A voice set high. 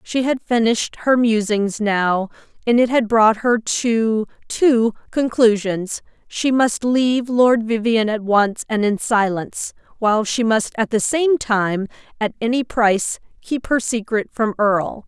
Yes: high, 225 Hz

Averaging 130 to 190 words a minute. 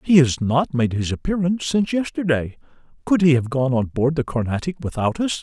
No: average, 200 wpm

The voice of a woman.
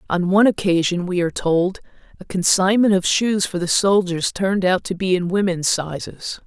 Yes: female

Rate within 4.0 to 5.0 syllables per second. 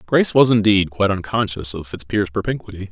No: 6.1 syllables/s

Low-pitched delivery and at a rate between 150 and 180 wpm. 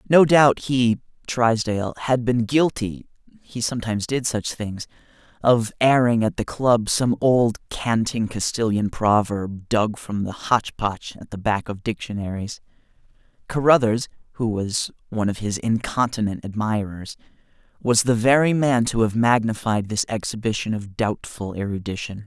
No: low, 110 Hz; slow, 135 wpm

